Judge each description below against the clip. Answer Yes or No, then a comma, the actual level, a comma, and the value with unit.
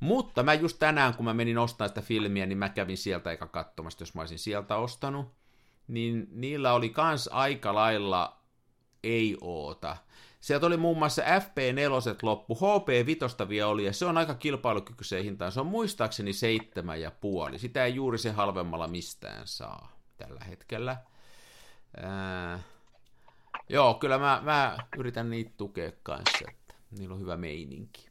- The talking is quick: Yes, fast, 160 wpm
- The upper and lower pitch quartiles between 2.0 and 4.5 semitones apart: No, average, 5.1 semitones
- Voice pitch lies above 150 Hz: No, low, 115 Hz